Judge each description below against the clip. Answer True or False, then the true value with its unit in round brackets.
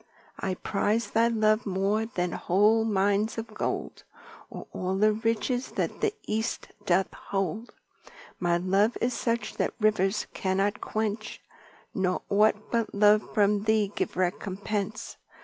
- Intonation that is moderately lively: False (2.2 semitones)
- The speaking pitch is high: True (210 Hz)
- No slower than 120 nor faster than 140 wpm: True (135 wpm)